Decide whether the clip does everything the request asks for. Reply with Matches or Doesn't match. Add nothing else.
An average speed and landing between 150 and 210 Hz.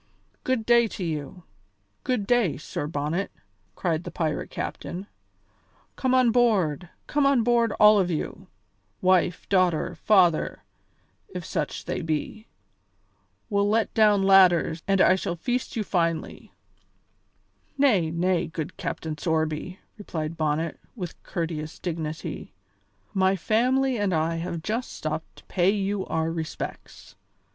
Doesn't match